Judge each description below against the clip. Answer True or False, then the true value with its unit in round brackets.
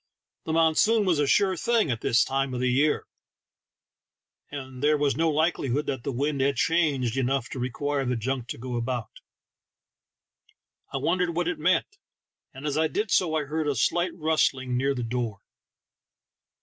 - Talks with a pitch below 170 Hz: True (140 Hz)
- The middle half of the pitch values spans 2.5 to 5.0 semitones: True (4.0 semitones)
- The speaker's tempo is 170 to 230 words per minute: True (175 wpm)